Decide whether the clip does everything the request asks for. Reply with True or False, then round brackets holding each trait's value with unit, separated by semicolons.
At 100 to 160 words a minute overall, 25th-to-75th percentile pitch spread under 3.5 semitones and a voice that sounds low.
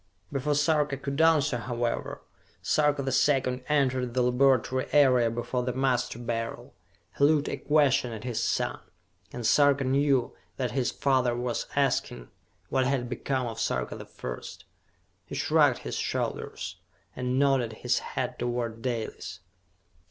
True (145 wpm; 2.4 semitones; 130 Hz)